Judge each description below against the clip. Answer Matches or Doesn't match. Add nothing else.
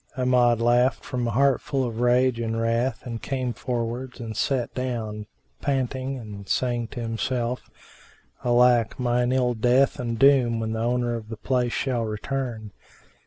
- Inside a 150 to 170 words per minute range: Matches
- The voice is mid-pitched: Doesn't match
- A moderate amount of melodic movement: Doesn't match